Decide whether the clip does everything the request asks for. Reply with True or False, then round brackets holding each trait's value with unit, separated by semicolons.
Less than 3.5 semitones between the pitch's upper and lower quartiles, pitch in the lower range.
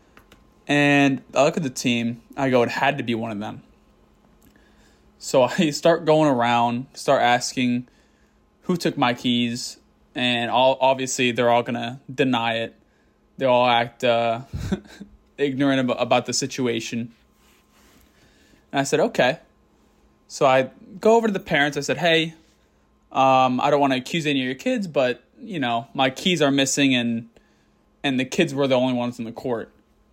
True (3.0 semitones; 130 Hz)